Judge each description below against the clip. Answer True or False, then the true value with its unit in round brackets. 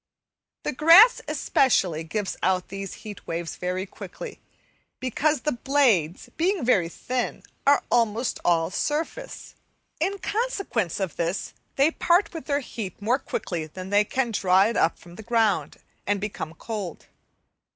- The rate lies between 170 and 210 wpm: False (145 wpm)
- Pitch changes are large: True (7.6 semitones)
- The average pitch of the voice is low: False (220 Hz)